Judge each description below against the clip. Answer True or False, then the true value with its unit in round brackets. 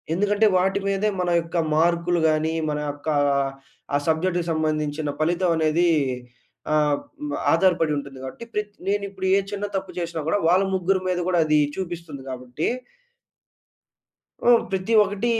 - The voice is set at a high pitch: False (170 Hz)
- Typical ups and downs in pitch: True (3.6 semitones)